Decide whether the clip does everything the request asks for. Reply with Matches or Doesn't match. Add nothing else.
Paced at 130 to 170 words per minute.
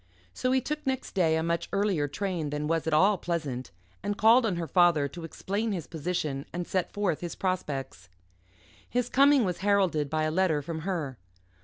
Doesn't match